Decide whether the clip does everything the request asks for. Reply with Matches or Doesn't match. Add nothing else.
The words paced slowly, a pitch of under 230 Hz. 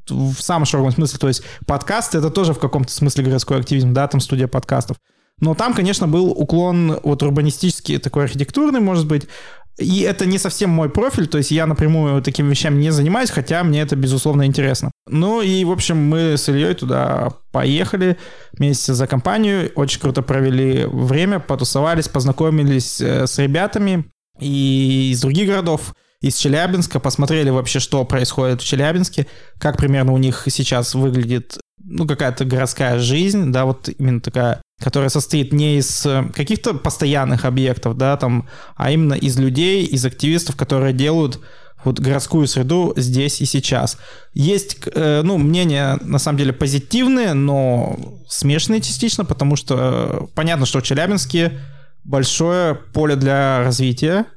Doesn't match